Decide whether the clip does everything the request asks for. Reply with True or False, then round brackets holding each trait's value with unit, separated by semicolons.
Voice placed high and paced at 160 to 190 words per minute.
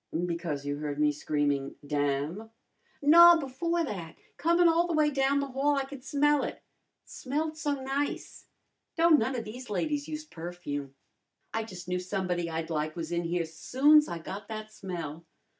True (215 Hz; 170 wpm)